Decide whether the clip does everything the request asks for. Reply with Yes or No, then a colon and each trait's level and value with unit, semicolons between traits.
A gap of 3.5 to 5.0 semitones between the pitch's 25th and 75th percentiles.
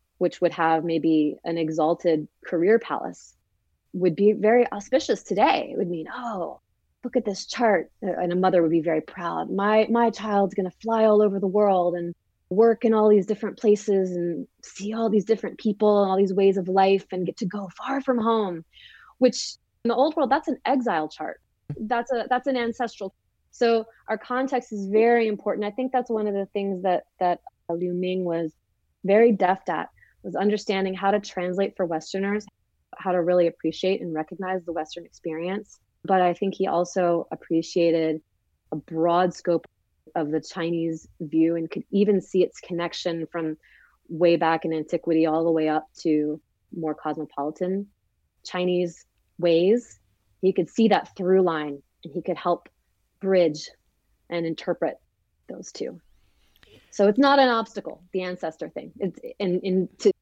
Yes: average, 4.1 semitones